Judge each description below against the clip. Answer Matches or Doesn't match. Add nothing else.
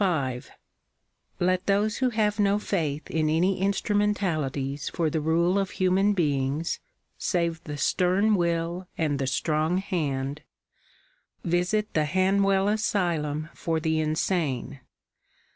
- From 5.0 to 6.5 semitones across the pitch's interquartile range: Doesn't match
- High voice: Doesn't match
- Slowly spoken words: Matches